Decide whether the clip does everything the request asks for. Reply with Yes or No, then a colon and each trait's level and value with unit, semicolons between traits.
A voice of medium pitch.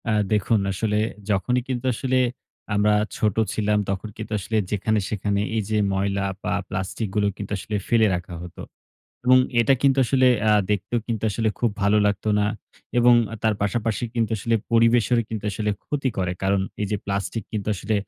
No: low, 105 Hz